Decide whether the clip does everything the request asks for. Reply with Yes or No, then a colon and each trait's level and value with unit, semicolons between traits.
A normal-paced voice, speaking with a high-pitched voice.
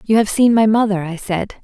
No: fast, 255 wpm; high, 210 Hz